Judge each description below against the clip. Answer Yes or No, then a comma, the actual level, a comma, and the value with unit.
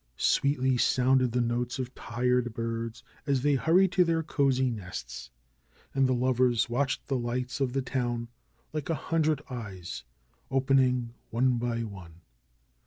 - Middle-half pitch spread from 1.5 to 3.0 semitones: Yes, narrow, 2.4 semitones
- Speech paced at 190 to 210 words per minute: No, average, 145 wpm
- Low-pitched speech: Yes, low, 125 Hz